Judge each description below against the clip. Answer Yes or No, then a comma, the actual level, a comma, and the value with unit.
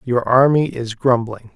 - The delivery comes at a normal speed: Yes, average, 155 wpm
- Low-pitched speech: Yes, low, 120 Hz